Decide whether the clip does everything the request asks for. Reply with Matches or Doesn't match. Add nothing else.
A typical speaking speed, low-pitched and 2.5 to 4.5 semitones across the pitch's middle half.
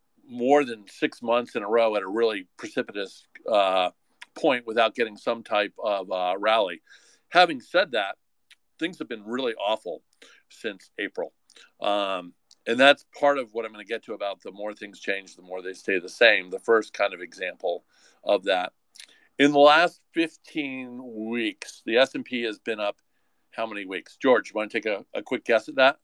Matches